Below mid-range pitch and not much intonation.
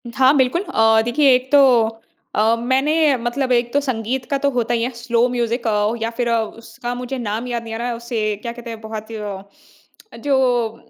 No: high, 240 Hz; narrow, 2.3 semitones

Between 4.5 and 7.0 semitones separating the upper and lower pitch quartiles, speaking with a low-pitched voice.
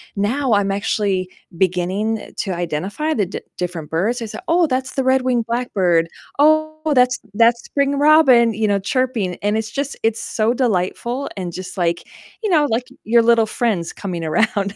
No: average, 5.2 semitones; high, 225 Hz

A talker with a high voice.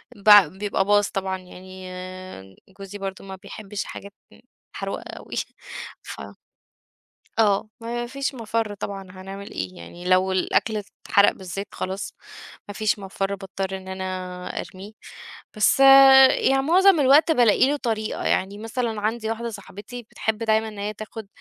Yes: high, 205 Hz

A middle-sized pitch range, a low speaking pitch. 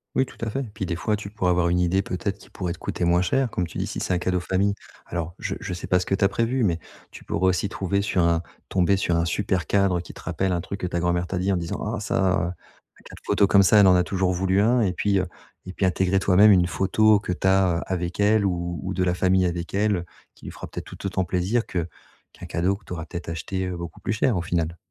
No: narrow, 2.1 semitones; very low, 95 Hz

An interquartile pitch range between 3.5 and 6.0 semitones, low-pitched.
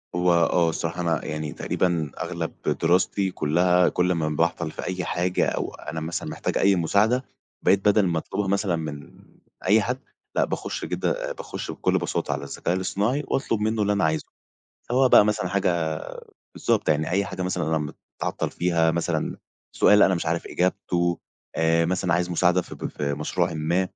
No: average, 2.9 semitones; very low, 90 Hz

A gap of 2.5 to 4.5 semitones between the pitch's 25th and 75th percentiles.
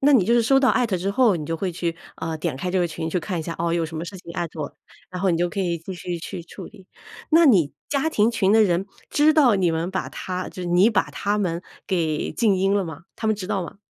Yes: average, 3.8 semitones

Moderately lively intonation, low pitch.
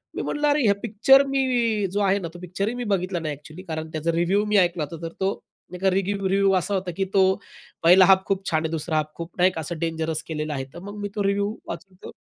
No: average, 3.5 semitones; high, 190 Hz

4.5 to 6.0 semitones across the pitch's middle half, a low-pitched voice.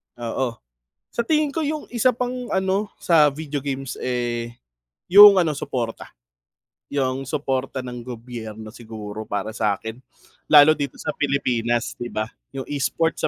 Yes: wide, 5.5 semitones; low, 130 Hz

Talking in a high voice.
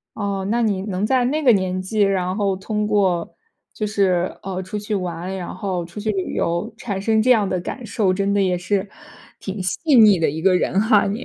Yes: high, 195 Hz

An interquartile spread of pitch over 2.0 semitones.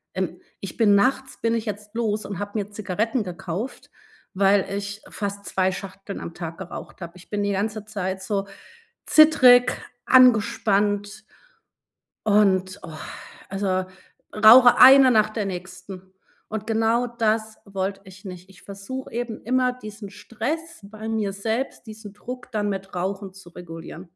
Yes: average, 2.7 semitones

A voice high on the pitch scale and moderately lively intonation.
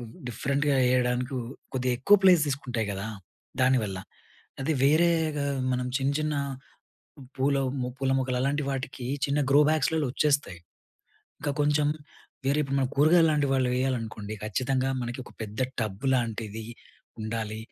No: low, 130 Hz; average, 3.2 semitones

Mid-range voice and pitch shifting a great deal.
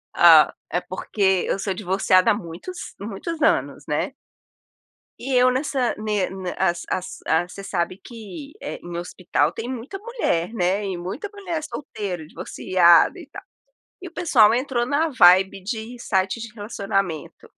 No: high, 210 Hz; wide, 5.7 semitones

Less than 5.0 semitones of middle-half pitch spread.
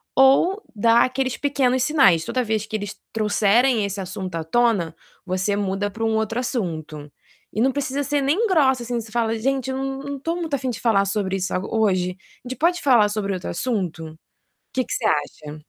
No: wide, 5.4 semitones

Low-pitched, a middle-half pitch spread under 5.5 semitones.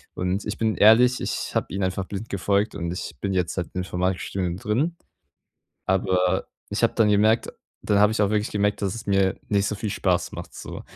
Yes: low, 100 Hz; narrow, 2.4 semitones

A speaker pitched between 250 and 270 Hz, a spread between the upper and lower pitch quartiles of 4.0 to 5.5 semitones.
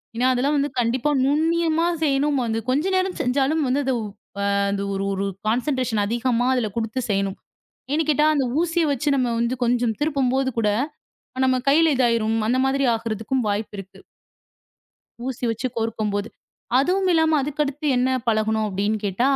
Yes: very high, 255 Hz; average, 4.6 semitones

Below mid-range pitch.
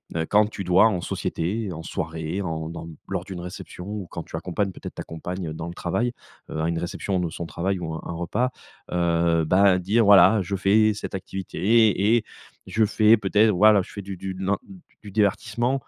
Yes: very low, 95 Hz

